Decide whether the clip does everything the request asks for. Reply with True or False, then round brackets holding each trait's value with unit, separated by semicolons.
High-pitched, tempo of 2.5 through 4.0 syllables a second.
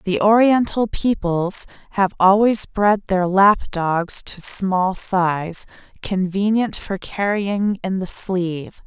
True (195 Hz; 3.3 syllables/s)